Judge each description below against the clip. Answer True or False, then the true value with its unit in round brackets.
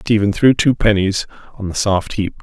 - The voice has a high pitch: False (105 Hz)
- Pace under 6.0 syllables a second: True (4.9 syllables/s)